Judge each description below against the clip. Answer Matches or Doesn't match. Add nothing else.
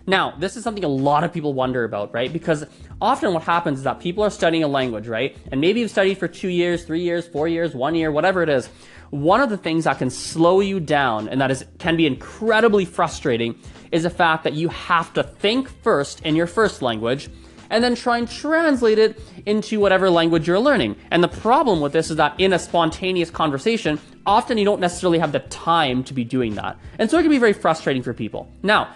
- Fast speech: Matches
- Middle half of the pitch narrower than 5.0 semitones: Doesn't match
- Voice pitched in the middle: Matches